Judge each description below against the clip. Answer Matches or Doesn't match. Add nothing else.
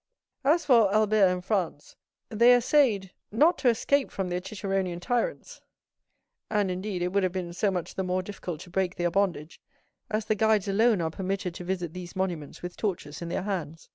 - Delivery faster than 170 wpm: Matches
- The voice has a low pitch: Doesn't match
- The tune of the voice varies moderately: Matches